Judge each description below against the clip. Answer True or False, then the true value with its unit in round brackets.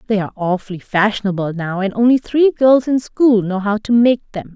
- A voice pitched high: True (215 Hz)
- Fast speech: True (210 wpm)